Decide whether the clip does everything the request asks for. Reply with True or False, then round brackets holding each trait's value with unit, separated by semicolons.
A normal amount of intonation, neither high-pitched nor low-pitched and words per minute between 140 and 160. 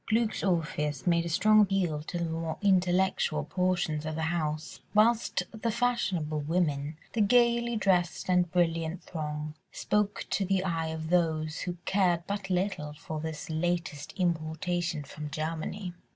True (3.6 semitones; 175 Hz; 150 wpm)